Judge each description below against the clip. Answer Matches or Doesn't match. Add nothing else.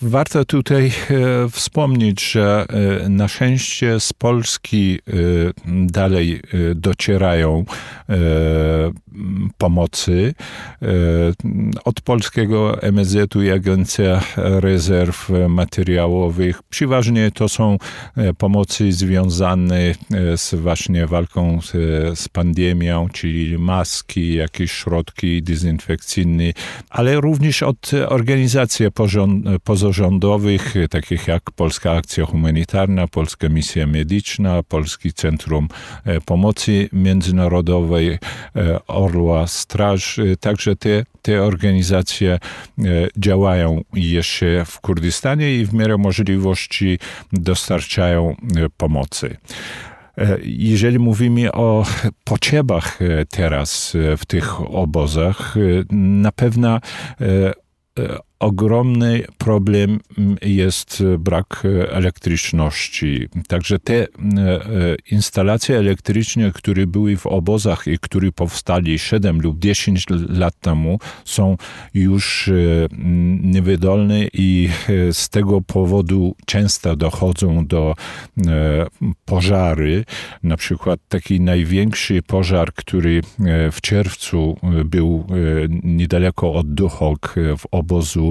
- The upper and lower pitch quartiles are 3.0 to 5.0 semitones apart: Matches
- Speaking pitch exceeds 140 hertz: Doesn't match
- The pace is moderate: Doesn't match